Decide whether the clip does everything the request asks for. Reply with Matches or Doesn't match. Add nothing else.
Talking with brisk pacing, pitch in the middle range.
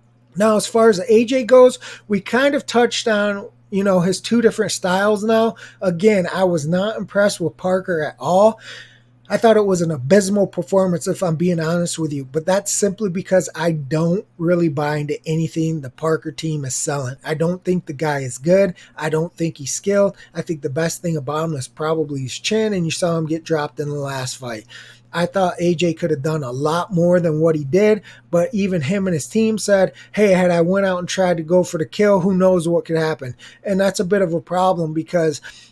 Matches